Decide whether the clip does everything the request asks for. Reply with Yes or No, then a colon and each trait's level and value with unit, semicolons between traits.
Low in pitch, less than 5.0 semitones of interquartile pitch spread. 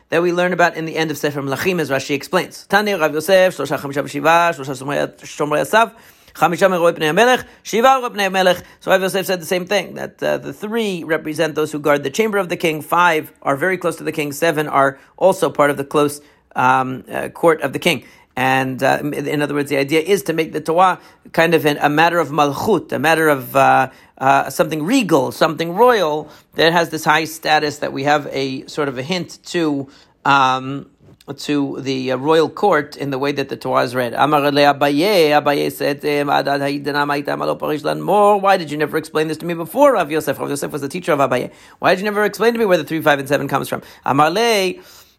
No: medium, 155 Hz; average, 3.7 semitones